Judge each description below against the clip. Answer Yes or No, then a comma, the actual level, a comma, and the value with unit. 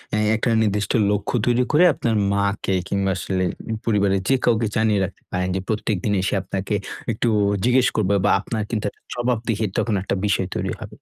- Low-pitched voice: Yes, low, 105 Hz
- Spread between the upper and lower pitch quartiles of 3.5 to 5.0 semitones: No, average, 2.7 semitones